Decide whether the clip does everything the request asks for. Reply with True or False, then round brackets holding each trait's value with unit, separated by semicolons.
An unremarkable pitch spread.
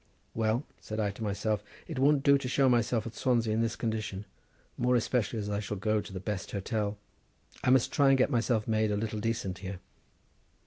True (3.0 semitones)